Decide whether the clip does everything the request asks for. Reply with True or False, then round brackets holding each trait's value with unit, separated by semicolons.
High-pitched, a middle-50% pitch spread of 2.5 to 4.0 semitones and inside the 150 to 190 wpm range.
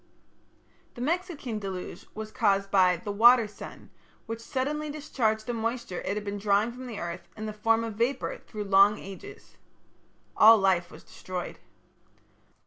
True (215 Hz; 3.3 semitones; 155 wpm)